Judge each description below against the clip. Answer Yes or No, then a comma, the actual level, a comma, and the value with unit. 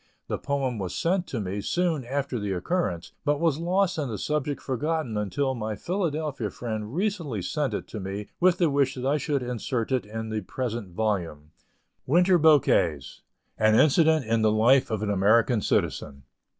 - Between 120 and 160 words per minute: No, average, 175 wpm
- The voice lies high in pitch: No, low, 125 Hz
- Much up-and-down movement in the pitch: Yes, wide, 6.1 semitones